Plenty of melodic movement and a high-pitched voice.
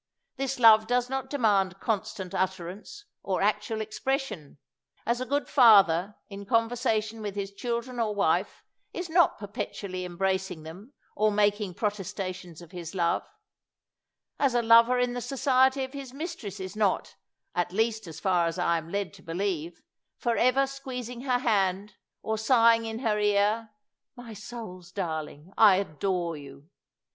No: average, 4.5 semitones; high, 210 Hz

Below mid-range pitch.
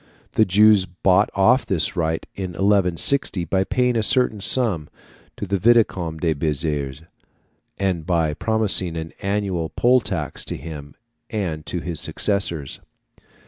Yes: very low, 95 Hz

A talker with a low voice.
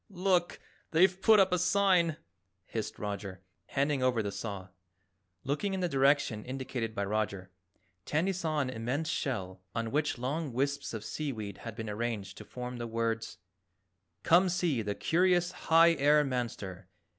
Yes: low, 130 Hz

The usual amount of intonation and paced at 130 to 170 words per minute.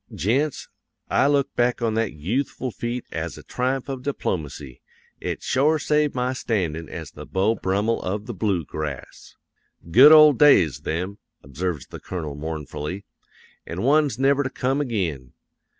No: wide, 8.2 semitones; average, 150 wpm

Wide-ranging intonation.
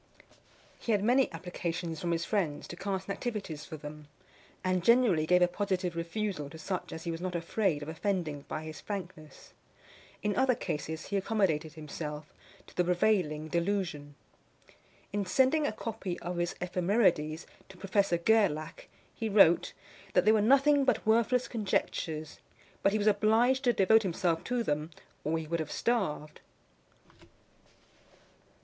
No: average, 5.0 semitones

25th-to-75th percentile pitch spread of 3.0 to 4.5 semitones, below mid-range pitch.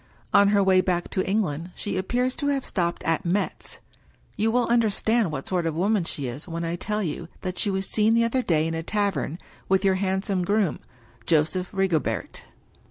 No: average, 3.8 semitones; high, 190 Hz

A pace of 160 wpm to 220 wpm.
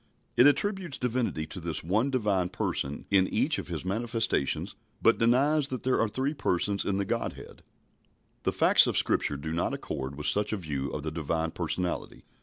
Yes: average, 185 wpm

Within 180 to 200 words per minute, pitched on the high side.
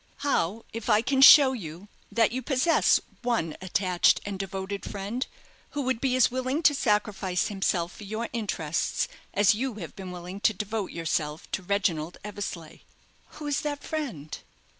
No: average, 160 wpm; high, 210 Hz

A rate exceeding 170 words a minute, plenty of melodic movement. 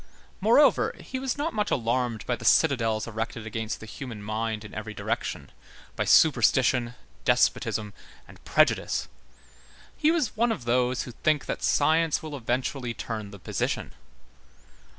No: average, 145 wpm; wide, 5.7 semitones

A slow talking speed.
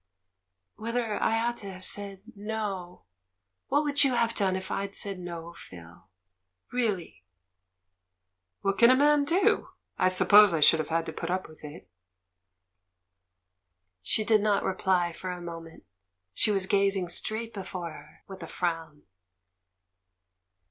No: average, 150 wpm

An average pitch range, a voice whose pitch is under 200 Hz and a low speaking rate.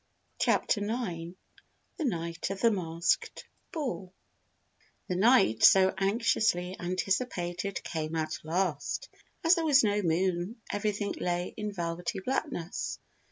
Yes: average, 3.8 semitones; high, 190 Hz; slow, 115 wpm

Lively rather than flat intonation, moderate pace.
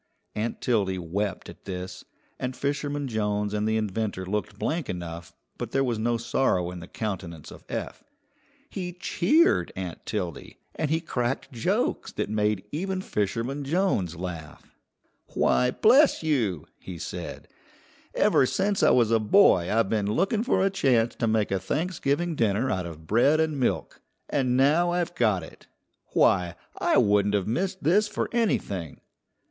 Yes: wide, 8.1 semitones; average, 160 wpm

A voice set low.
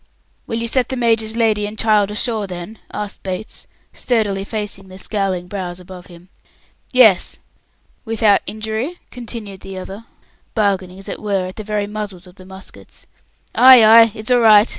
No: high, 210 Hz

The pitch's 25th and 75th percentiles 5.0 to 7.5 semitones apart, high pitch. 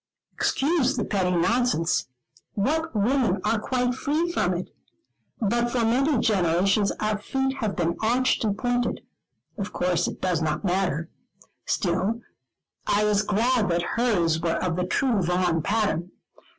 Yes: wide, 5.4 semitones; high, 210 Hz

